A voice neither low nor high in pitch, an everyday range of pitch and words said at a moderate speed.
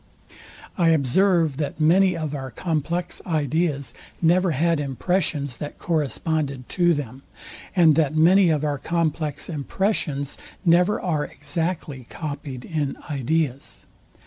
No: medium, 155 Hz; average, 3.2 semitones; slow, 120 wpm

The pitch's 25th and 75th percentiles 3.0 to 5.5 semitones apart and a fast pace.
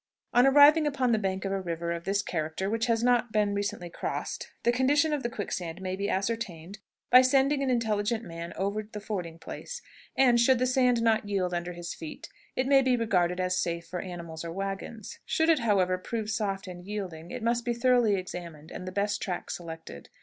Yes: average, 5.1 semitones; fast, 210 wpm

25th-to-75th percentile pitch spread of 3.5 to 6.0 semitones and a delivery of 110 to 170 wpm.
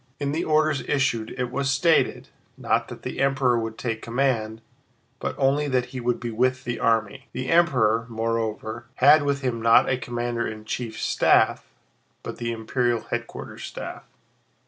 No: average, 3.0 semitones; average, 165 wpm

